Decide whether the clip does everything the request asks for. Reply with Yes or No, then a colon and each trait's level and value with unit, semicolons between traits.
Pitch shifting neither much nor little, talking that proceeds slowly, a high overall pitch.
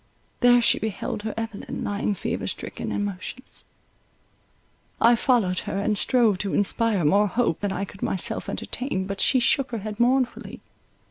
No: average, 3.3 semitones; average, 160 wpm; high, 210 Hz